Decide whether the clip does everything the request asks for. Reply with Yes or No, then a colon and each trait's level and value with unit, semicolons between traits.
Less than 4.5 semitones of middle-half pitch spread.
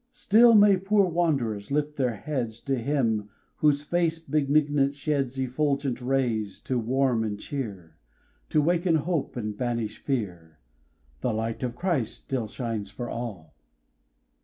No: average, 5.2 semitones